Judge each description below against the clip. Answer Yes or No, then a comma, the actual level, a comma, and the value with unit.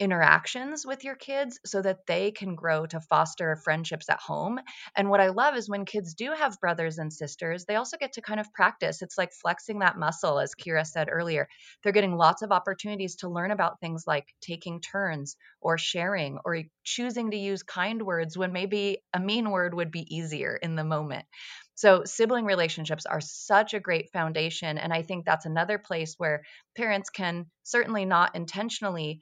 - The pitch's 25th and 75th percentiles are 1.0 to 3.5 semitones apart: No, average, 4.2 semitones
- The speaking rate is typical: Yes, average, 190 wpm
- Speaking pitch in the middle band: Yes, medium, 180 Hz